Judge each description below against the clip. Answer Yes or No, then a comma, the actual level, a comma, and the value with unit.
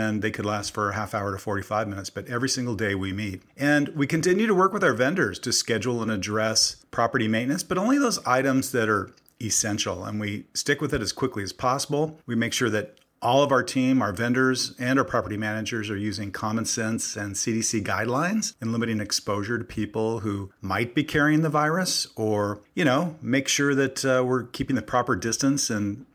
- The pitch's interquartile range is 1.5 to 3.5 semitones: No, average, 4.3 semitones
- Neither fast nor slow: No, fast, 210 wpm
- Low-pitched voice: Yes, low, 115 Hz